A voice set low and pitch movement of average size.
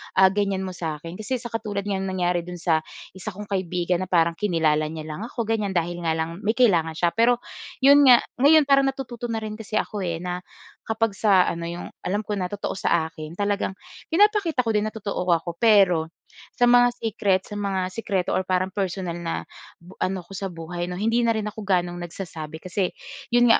No: high, 190 Hz; average, 4.0 semitones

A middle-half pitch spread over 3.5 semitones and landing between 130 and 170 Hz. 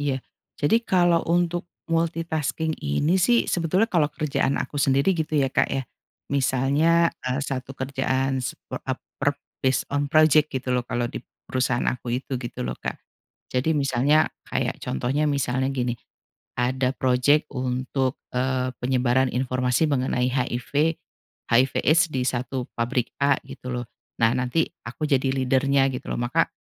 No: average, 3.2 semitones; low, 135 Hz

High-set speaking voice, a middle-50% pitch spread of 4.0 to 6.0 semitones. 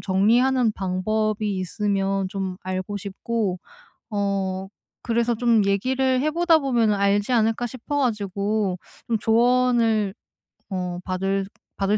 No: high, 210 Hz; average, 3.4 semitones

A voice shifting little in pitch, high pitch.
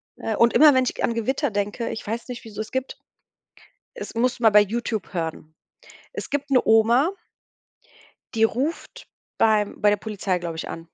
No: average, 3.6 semitones; high, 225 Hz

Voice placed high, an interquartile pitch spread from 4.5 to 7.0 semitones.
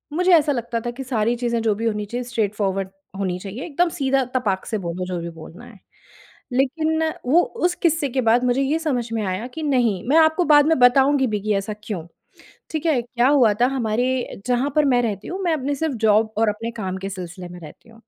Yes: high, 240 Hz; average, 4.9 semitones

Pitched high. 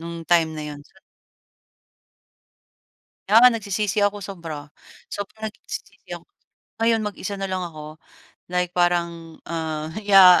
No: medium, 180 Hz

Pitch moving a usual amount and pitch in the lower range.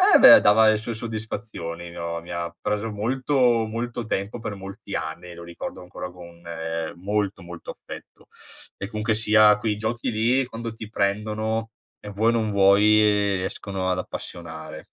Yes: average, 3.6 semitones; low, 105 Hz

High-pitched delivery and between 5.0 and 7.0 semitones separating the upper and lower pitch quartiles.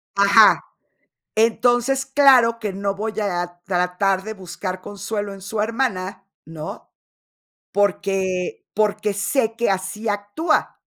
No: high, 205 Hz; average, 2.8 semitones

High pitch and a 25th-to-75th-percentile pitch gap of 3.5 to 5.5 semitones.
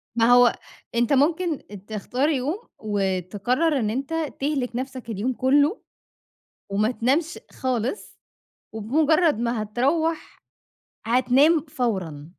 Yes: very high, 250 Hz; average, 5.0 semitones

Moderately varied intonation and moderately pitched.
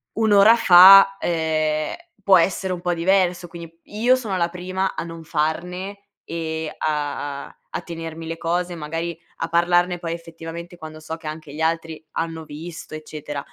No: narrow, 2.1 semitones; medium, 165 Hz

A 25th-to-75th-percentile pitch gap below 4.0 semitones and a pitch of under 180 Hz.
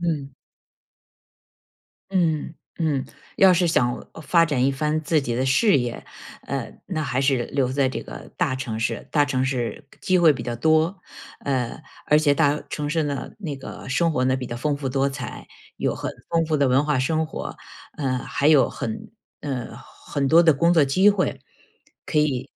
Yes: average, 3.3 semitones; medium, 140 Hz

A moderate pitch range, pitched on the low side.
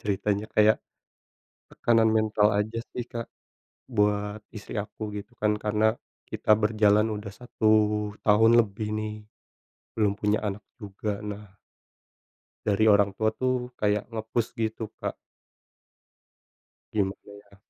No: narrow, 1.1 semitones; low, 105 Hz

